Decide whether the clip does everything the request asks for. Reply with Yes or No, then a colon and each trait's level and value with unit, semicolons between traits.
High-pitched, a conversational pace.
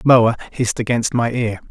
No: low, 115 Hz; average, 175 wpm